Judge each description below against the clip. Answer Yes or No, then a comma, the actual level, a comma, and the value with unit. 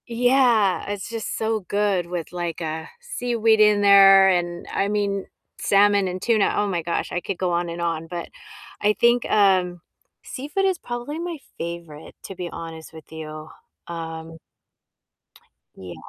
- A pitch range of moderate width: Yes, average, 4.3 semitones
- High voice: Yes, high, 195 Hz